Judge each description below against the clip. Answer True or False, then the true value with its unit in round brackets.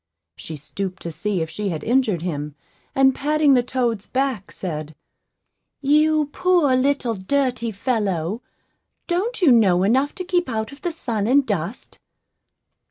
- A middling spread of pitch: False (6.7 semitones)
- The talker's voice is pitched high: True (240 Hz)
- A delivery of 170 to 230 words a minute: False (150 wpm)